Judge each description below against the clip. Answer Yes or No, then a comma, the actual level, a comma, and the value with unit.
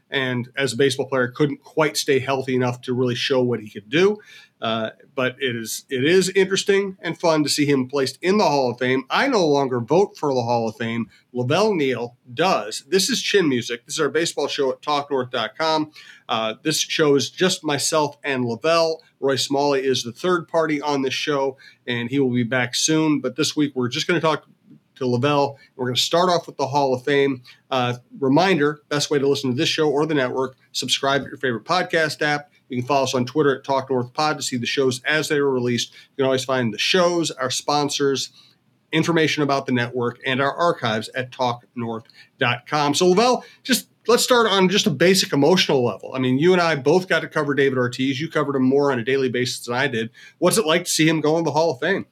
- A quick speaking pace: Yes, fast, 225 wpm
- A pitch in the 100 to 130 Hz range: No, medium, 140 Hz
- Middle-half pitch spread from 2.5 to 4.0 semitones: Yes, average, 3.6 semitones